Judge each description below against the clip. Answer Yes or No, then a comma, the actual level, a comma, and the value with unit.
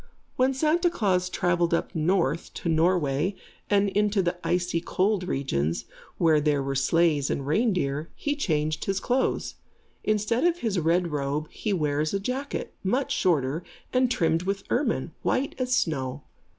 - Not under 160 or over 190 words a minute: No, average, 150 wpm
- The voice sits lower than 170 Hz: No, medium, 175 Hz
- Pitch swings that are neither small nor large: No, wide, 5.7 semitones